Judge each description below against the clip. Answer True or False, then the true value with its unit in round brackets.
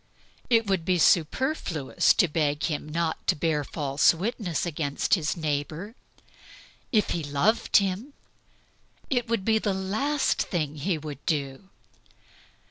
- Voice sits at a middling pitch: True (170 Hz)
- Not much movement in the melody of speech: False (5.5 semitones)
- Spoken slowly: True (130 wpm)